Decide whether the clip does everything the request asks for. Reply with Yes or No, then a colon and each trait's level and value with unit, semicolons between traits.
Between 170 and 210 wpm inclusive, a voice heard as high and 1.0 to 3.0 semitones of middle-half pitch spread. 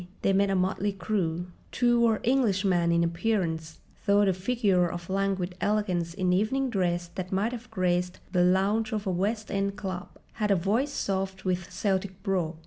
Yes: average, 175 wpm; high, 195 Hz; average, 2.7 semitones